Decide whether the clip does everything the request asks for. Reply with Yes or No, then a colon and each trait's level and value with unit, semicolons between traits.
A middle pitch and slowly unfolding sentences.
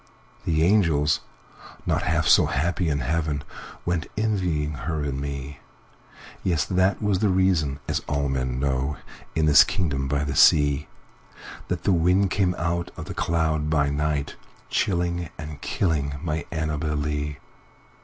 No: very low, 75 Hz; slow, 130 wpm